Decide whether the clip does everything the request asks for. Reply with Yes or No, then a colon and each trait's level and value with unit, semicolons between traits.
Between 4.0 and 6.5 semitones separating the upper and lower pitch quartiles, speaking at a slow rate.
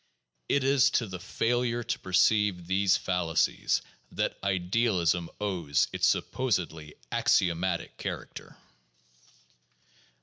Yes: average, 4.8 semitones; slow, 95 wpm